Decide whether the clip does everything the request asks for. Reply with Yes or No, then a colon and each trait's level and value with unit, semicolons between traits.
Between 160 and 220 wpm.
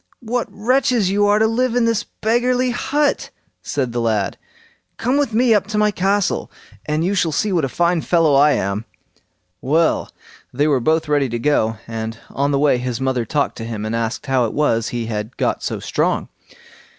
Yes: average, 200 wpm